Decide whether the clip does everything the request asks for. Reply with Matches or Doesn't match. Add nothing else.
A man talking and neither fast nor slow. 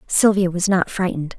Doesn't match